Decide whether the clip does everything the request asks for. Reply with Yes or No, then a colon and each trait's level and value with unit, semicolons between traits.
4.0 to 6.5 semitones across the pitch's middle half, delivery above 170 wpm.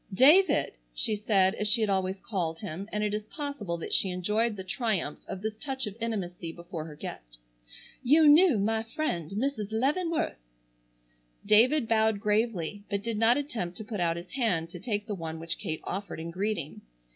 Yes: average, 4.3 semitones; average, 185 wpm